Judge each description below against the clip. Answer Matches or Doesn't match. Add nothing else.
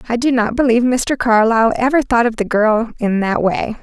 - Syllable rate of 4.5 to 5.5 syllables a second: Matches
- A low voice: Doesn't match